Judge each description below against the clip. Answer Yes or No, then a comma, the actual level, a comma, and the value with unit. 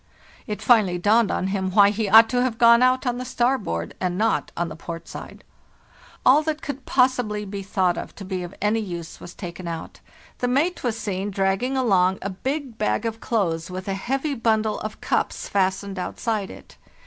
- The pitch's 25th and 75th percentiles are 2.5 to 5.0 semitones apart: Yes, average, 4.7 semitones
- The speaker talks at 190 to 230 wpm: Yes, average, 195 wpm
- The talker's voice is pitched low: No, high, 210 Hz